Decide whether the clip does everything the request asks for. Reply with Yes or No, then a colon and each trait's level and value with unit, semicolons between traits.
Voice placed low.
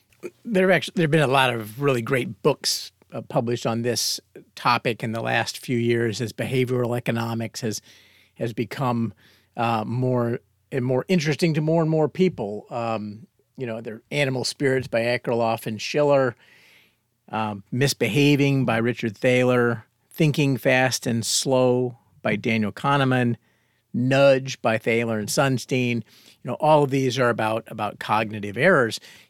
Yes: low, 120 Hz